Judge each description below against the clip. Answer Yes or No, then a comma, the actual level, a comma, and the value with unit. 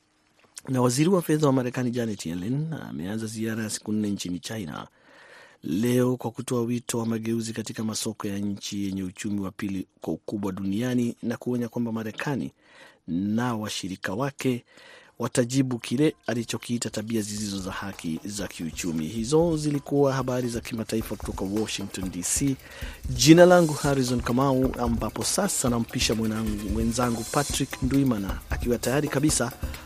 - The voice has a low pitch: Yes, low, 115 Hz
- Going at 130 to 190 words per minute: Yes, average, 135 wpm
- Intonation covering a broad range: No, average, 3.7 semitones